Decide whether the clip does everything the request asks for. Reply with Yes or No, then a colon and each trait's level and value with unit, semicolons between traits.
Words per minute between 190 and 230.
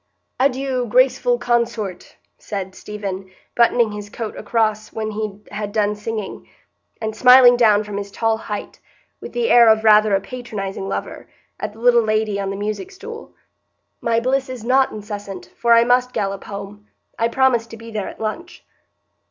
No: average, 170 wpm